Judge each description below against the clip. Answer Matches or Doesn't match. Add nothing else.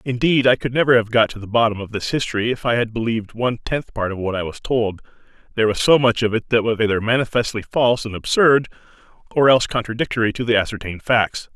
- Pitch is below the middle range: Matches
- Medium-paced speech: Doesn't match